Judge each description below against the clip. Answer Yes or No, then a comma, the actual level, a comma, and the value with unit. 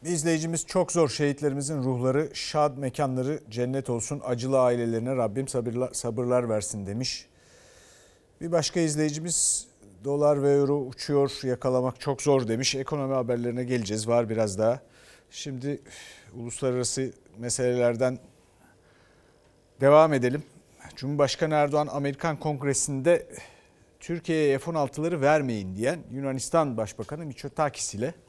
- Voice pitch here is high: No, low, 135 Hz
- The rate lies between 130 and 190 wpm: No, average, 110 wpm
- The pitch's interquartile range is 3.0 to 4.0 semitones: Yes, average, 3.3 semitones